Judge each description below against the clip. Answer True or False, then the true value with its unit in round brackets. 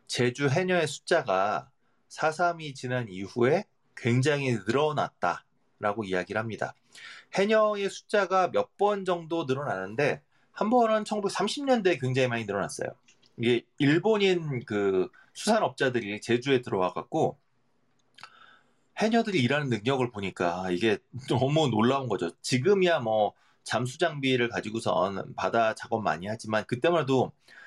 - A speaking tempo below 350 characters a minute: True (285 characters per minute)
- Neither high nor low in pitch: False (130 Hz)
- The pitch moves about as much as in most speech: False (7.0 semitones)